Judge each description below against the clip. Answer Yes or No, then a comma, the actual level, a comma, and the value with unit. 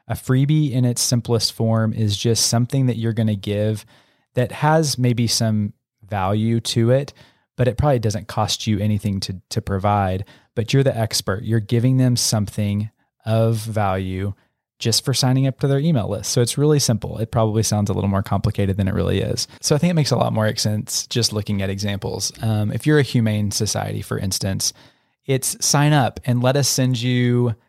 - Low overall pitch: Yes, low, 115 Hz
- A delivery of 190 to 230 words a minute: Yes, average, 200 wpm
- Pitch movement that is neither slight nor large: Yes, average, 3.2 semitones